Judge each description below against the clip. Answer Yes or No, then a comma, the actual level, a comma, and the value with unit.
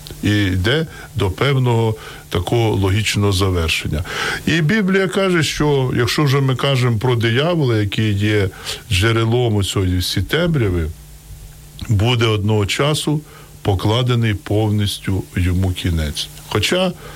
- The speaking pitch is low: Yes, low, 110 Hz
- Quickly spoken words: No, average, 110 wpm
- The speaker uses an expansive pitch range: Yes, wide, 5.9 semitones